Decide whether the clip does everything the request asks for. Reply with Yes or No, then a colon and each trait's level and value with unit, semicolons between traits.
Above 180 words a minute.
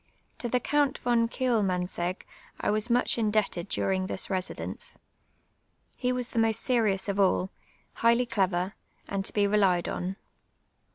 No: average, 145 wpm